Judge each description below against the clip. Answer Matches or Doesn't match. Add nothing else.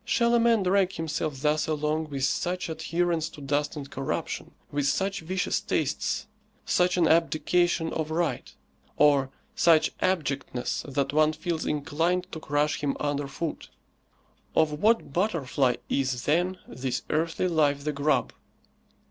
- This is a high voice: Doesn't match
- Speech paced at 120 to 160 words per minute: Matches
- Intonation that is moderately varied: Matches